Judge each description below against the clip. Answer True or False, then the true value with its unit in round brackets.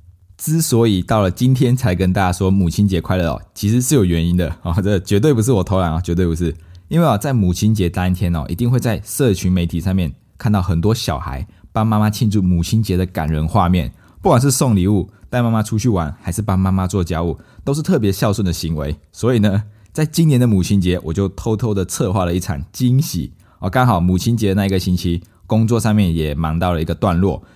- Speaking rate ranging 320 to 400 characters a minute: True (335 characters per minute)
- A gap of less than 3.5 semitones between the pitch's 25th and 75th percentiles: False (3.9 semitones)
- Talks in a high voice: False (95 Hz)